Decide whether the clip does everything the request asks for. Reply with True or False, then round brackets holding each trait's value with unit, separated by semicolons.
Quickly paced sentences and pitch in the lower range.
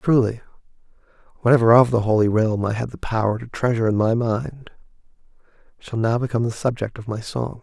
False (180 wpm; 115 Hz)